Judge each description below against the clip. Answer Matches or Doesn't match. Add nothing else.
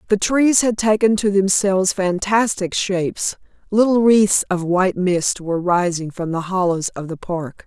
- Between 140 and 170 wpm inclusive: Matches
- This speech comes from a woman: Matches